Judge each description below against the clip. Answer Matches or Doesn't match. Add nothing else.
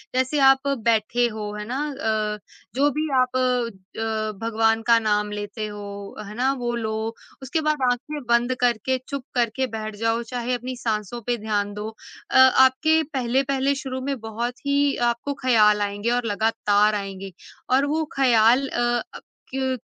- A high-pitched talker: Matches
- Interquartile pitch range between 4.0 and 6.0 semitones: Doesn't match